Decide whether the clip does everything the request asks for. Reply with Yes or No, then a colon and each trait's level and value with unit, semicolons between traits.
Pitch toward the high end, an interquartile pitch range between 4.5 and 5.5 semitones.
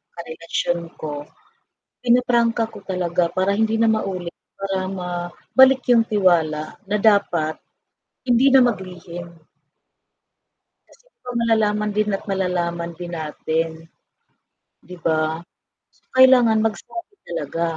Yes: high, 195 Hz; average, 5.0 semitones